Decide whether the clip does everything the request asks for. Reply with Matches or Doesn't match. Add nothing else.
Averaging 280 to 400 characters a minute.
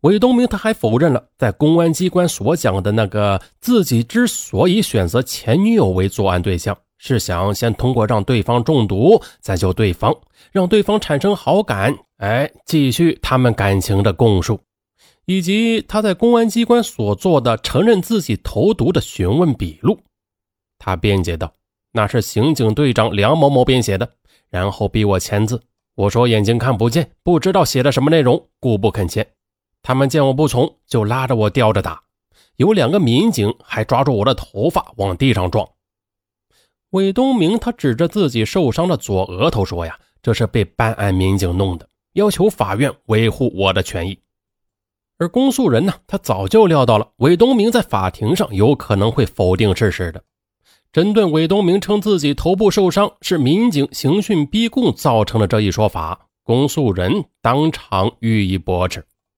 Doesn't match